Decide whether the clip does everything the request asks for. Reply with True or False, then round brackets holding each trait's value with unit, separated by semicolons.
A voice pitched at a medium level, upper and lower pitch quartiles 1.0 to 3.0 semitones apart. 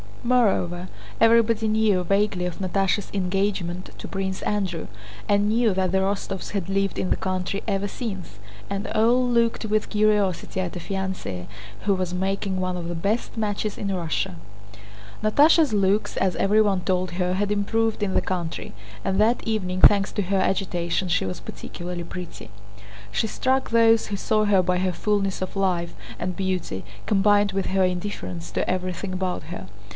False (195 Hz; 2.4 semitones)